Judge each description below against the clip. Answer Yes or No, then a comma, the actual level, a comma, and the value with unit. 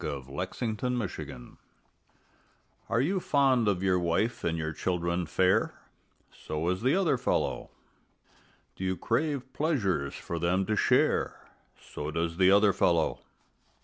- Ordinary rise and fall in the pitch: No, wide, 6.5 semitones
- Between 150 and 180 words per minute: No, slow, 135 wpm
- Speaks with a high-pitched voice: No, very low, 95 Hz